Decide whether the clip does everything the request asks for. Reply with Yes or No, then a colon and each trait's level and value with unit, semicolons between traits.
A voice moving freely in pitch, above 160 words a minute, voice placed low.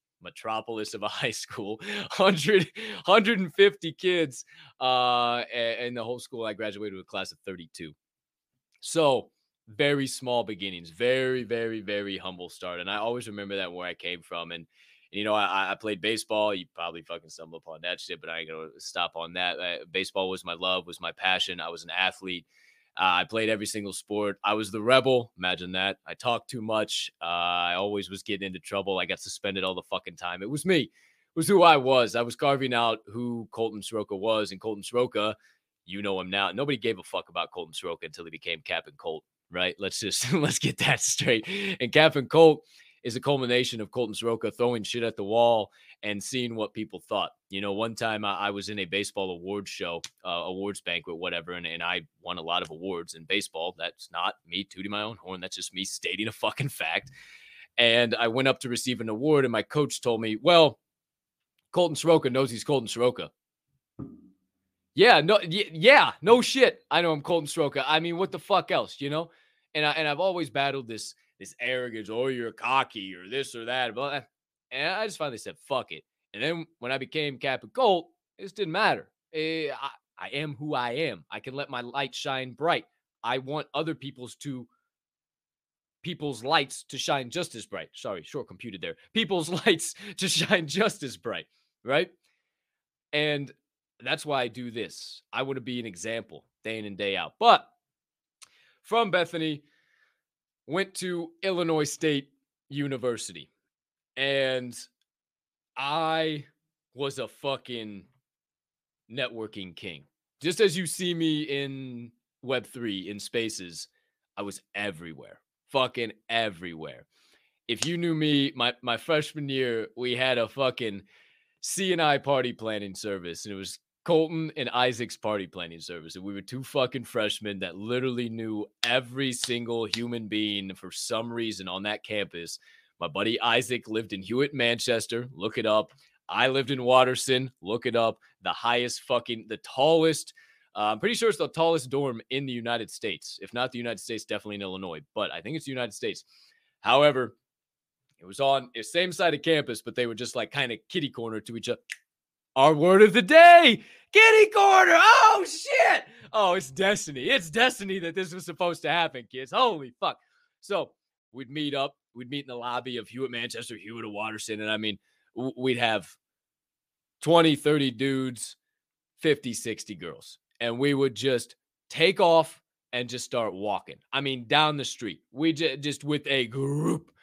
Yes: wide, 5.8 semitones; average, 180 wpm; low, 125 Hz